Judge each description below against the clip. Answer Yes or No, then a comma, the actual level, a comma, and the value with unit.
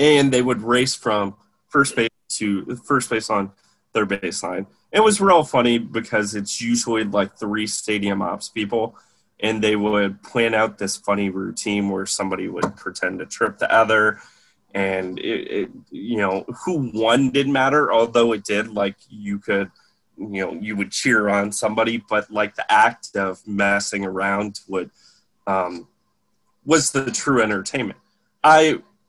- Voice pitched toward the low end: Yes, low, 110 Hz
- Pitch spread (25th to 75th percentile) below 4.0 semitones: Yes, average, 3.4 semitones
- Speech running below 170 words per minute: Yes, average, 160 wpm